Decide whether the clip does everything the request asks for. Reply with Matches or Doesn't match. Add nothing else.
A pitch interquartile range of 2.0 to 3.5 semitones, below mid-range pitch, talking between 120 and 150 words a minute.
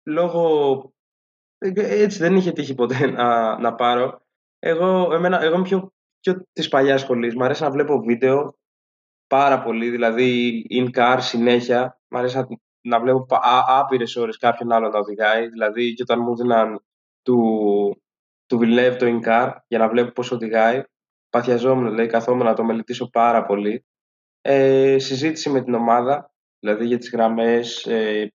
Matches